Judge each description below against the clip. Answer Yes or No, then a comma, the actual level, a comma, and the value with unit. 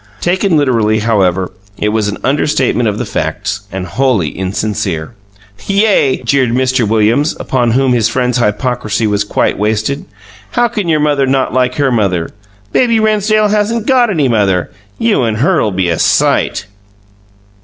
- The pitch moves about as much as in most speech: No, wide, 5.9 semitones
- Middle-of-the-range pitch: No, low, 125 Hz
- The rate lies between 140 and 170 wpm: Yes, average, 155 wpm